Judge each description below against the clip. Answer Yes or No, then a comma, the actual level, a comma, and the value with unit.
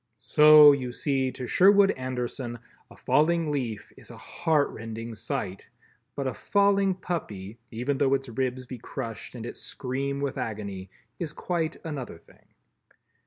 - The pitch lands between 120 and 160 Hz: Yes, low, 135 Hz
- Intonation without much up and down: No, average, 4.4 semitones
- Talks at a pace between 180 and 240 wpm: No, average, 150 wpm